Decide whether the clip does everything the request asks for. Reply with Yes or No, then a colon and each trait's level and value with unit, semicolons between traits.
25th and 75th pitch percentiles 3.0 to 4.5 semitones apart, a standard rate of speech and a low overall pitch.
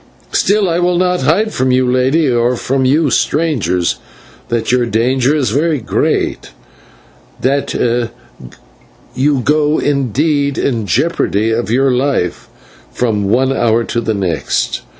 No: average, 4.1 semitones; slow, 130 wpm; low, 130 Hz